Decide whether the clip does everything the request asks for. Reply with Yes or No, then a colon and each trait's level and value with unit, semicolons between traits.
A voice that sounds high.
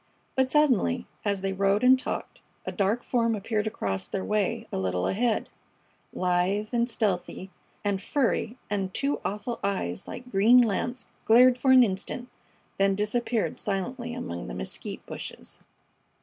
Yes: high, 210 Hz